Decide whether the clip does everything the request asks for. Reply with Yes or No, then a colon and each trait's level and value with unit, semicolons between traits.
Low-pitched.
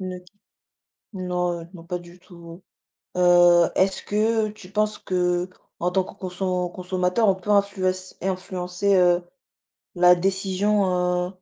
No: medium, 180 Hz